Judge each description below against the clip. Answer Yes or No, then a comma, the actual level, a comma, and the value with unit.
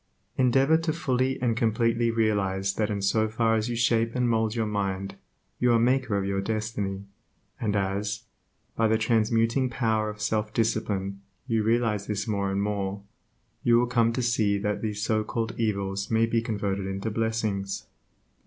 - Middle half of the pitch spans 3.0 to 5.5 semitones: No, narrow, 2.4 semitones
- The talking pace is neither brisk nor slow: Yes, average, 175 wpm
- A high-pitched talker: No, low, 110 Hz